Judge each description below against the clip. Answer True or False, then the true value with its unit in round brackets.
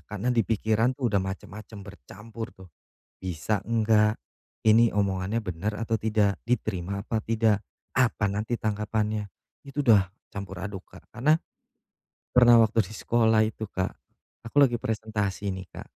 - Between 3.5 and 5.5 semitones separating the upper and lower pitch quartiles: False (2.4 semitones)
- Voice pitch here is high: False (110 Hz)